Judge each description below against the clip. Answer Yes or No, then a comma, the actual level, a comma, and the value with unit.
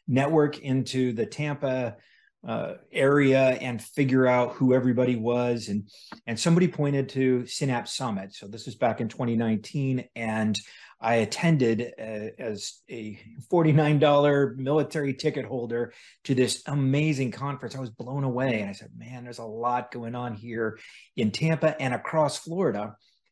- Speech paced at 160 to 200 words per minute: No, average, 150 wpm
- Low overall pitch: Yes, low, 125 Hz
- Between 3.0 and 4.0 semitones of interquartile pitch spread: Yes, average, 3.4 semitones